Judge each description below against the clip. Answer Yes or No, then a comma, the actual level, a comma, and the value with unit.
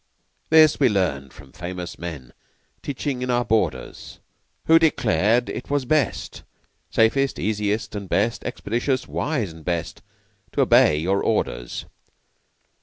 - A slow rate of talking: Yes, slow, 125 wpm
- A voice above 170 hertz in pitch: No, low, 110 Hz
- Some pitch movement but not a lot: No, wide, 6.4 semitones